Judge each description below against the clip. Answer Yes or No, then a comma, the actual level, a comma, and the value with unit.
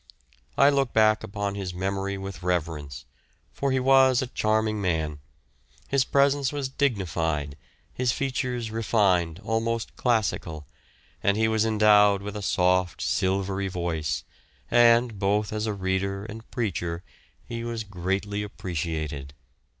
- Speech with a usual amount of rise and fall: Yes, average, 4.3 semitones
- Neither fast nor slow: No, slow, 130 wpm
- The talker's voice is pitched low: Yes, low, 100 Hz